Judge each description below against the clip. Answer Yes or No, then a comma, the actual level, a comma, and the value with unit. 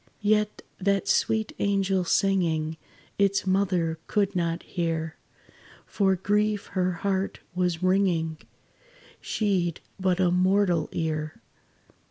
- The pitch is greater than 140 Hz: Yes, medium, 185 Hz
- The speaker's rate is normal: No, slow, 110 wpm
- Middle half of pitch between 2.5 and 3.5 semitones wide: Yes, average, 2.9 semitones